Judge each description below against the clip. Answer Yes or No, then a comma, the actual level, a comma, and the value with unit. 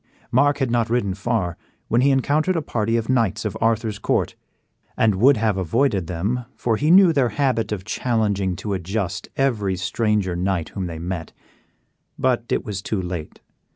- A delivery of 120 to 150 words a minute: No, average, 180 wpm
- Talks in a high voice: No, low, 110 Hz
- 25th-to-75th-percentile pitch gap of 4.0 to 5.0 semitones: Yes, average, 4.6 semitones